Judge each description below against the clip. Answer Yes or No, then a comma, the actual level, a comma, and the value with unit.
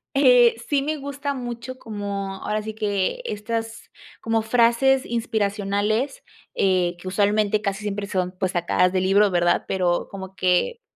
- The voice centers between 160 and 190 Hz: No, high, 210 Hz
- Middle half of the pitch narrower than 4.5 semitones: Yes, average, 3.6 semitones